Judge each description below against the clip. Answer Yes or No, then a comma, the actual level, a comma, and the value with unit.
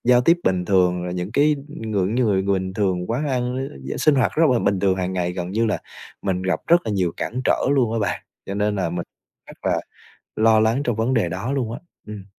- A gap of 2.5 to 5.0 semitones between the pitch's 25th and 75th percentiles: Yes, average, 4.7 semitones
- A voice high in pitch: No, low, 105 Hz